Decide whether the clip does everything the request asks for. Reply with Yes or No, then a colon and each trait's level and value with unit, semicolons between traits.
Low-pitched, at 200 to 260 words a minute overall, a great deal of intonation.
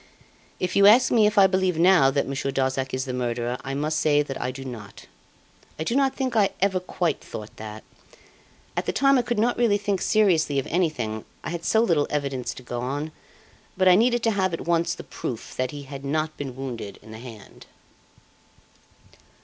No: medium, 155 Hz; fast, 205 wpm; wide, 7.1 semitones